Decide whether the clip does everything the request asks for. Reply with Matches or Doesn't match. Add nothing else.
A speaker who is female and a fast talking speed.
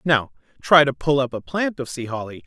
Doesn't match